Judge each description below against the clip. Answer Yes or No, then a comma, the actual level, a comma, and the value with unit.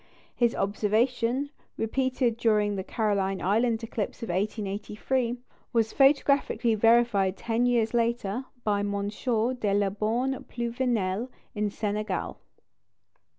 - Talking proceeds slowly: Yes, slow, 110 wpm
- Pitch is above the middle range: Yes, high, 225 Hz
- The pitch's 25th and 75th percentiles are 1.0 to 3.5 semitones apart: Yes, average, 2.8 semitones